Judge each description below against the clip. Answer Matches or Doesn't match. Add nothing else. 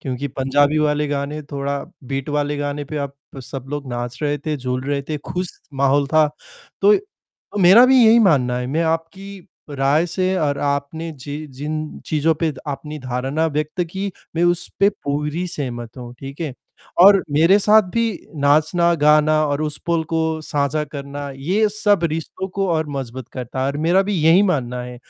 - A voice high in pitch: Doesn't match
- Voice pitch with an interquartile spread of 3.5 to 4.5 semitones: Doesn't match